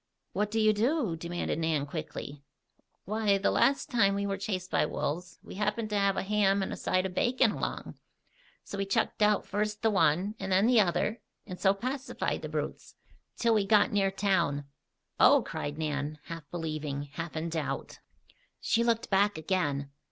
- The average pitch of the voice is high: Yes, high, 195 Hz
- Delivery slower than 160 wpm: No, average, 180 wpm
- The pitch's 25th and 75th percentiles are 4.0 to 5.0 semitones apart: Yes, average, 4.3 semitones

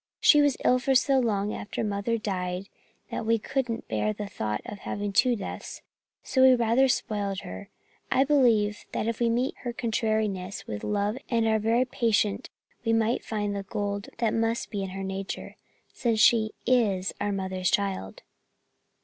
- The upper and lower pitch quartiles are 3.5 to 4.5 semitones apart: No, average, 3.0 semitones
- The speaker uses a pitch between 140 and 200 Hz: No, high, 215 Hz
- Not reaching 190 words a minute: Yes, average, 175 wpm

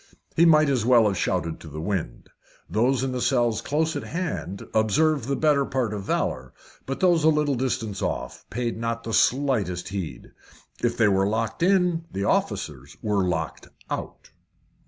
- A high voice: No, low, 115 Hz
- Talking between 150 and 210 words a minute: Yes, average, 175 wpm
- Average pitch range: No, wide, 6.3 semitones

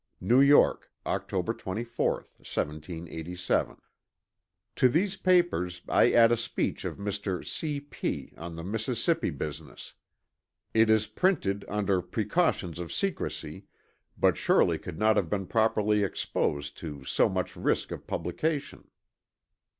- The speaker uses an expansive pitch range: Yes, wide, 6.0 semitones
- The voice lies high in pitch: No, low, 105 Hz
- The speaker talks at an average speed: No, slow, 125 wpm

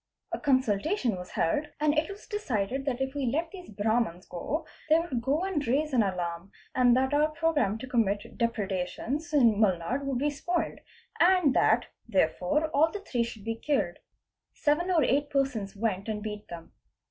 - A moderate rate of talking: Yes, average, 185 wpm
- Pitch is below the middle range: No, very high, 260 Hz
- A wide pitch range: Yes, wide, 6.3 semitones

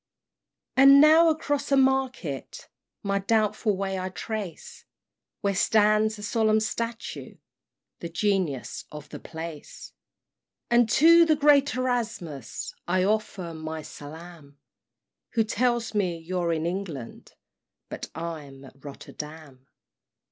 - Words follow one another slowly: Yes, slow, 120 wpm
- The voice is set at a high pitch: Yes, high, 200 Hz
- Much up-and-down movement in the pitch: Yes, wide, 6.6 semitones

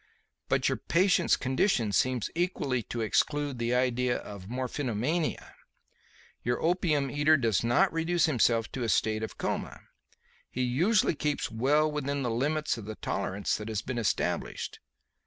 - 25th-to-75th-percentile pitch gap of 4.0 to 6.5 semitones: Yes, average, 4.8 semitones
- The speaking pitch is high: No, low, 130 Hz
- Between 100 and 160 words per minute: Yes, average, 150 wpm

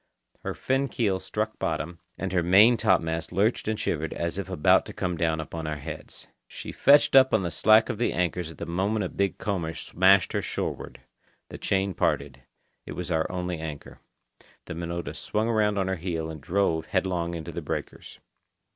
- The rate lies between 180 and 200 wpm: Yes, average, 190 wpm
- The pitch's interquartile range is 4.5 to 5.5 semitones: No, average, 3.3 semitones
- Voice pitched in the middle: No, very low, 90 Hz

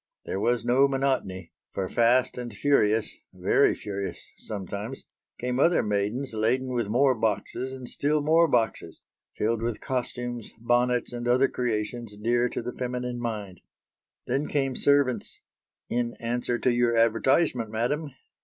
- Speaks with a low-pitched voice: Yes, low, 120 Hz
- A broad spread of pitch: No, narrow, 2.6 semitones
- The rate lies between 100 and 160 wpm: Yes, average, 140 wpm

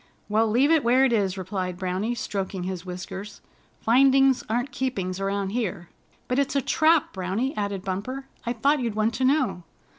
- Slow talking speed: No, average, 175 wpm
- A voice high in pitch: Yes, high, 220 Hz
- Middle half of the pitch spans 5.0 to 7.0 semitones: Yes, wide, 5.4 semitones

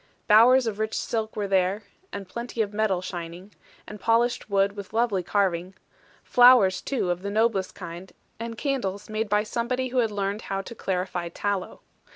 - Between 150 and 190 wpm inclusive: Yes, average, 175 wpm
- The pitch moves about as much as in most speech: Yes, average, 3.3 semitones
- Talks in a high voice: Yes, high, 205 Hz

